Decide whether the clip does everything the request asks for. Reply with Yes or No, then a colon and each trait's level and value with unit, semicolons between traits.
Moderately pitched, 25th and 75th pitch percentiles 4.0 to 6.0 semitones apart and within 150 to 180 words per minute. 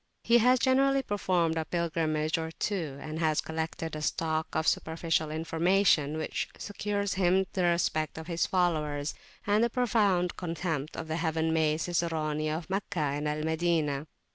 No: medium, 165 Hz; average, 2.9 semitones; average, 165 wpm